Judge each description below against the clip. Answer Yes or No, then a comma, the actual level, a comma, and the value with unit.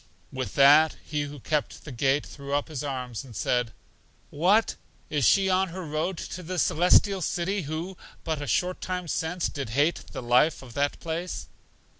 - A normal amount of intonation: Yes, average, 4.3 semitones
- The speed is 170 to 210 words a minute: Yes, average, 180 wpm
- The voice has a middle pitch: Yes, medium, 155 Hz